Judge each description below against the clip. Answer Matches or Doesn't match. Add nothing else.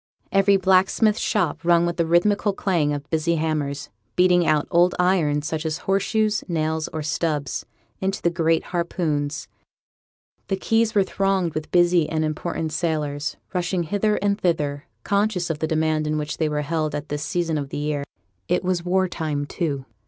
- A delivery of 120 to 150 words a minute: Doesn't match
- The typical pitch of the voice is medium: Matches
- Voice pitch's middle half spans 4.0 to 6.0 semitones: Doesn't match